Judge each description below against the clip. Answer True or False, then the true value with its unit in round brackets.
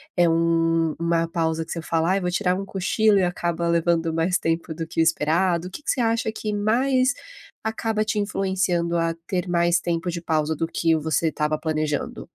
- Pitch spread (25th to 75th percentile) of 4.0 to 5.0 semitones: False (2.6 semitones)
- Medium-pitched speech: True (170 Hz)